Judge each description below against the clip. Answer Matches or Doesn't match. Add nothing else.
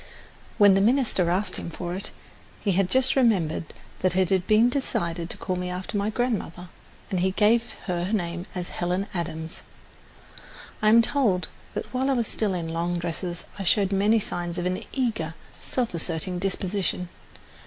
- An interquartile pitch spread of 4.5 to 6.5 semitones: Doesn't match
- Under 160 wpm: Doesn't match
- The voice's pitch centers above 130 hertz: Matches